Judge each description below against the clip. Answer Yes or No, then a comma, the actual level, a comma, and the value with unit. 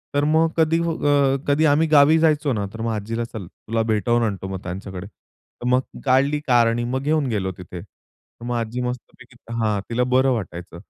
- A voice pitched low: Yes, low, 120 Hz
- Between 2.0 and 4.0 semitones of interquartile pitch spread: No, average, 4.9 semitones